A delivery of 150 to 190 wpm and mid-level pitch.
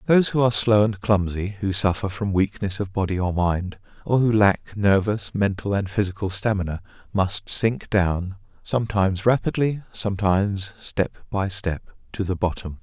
No: average, 160 wpm; low, 100 Hz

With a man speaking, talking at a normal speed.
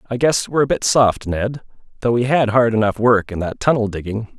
No: male; fast, 235 wpm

